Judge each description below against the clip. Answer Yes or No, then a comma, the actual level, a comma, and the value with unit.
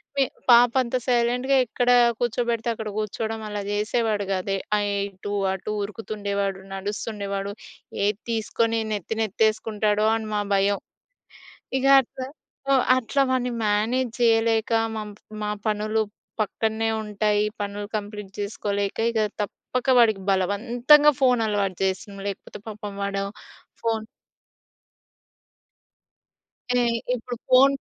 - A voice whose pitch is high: Yes, high, 215 Hz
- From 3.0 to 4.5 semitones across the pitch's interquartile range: No, narrow, 2.5 semitones